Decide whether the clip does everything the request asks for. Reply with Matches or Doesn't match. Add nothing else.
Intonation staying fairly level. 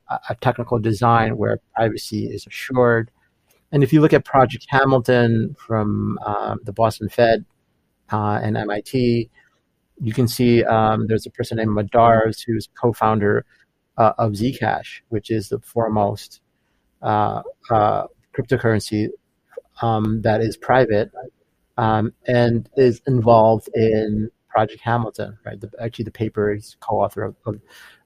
Matches